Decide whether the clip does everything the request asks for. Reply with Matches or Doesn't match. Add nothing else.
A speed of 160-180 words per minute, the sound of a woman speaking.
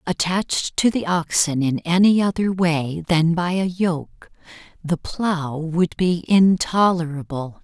Doesn't match